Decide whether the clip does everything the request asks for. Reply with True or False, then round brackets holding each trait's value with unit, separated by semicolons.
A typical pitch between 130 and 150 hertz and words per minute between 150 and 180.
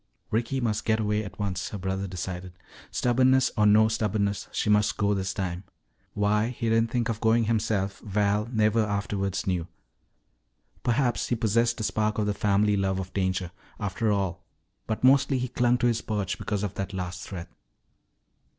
False (105 Hz; 175 wpm)